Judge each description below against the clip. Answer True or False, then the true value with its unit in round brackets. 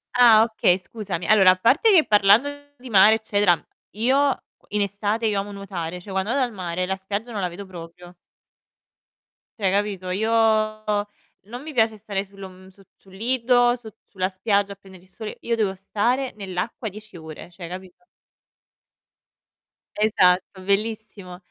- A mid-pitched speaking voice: False (205 Hz)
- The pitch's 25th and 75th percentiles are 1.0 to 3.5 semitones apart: True (2.9 semitones)